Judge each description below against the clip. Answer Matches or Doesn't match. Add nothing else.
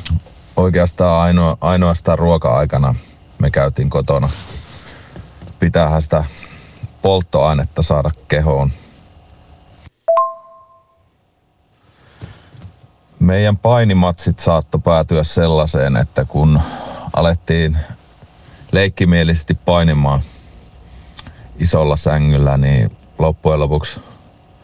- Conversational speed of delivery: Doesn't match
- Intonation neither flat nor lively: Matches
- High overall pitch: Doesn't match